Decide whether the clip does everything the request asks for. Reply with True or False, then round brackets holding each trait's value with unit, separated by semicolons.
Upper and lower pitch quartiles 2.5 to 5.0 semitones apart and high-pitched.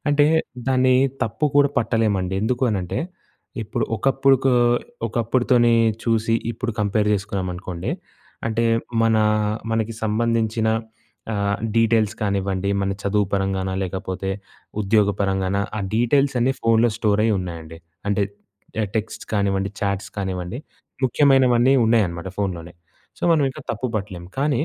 False (3.3 semitones; 110 Hz)